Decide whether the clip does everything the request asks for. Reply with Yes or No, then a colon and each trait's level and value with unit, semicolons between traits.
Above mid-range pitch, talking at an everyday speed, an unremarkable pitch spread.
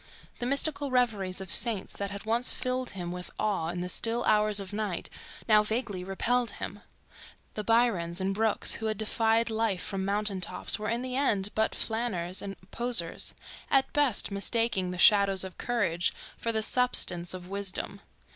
Yes: high, 210 Hz; average, 175 wpm; average, 3.5 semitones